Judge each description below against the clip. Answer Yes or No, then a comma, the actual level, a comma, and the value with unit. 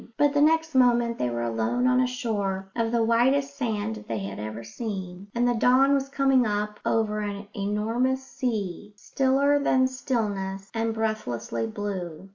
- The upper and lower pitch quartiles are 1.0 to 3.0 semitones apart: No, average, 4.8 semitones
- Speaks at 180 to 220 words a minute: No, average, 170 wpm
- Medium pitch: No, high, 225 Hz